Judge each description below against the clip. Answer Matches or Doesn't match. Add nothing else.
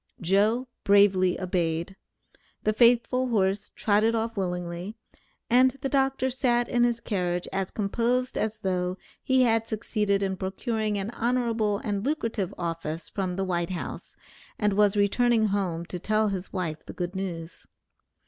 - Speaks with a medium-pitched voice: Doesn't match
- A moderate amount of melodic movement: Matches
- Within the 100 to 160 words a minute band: Matches